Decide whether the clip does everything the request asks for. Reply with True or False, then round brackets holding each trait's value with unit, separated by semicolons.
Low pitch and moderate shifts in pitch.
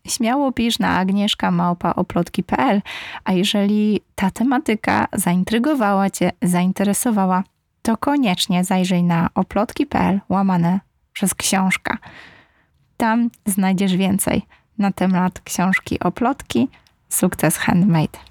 False (195 Hz; 3.2 semitones)